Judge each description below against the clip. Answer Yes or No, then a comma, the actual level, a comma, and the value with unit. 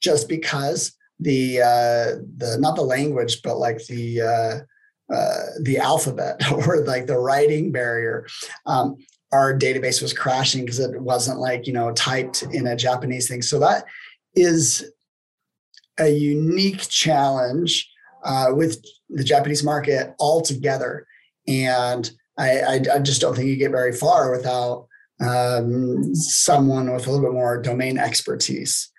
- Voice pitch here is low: Yes, low, 130 Hz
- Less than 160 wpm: Yes, average, 145 wpm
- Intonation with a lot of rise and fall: No, average, 3.1 semitones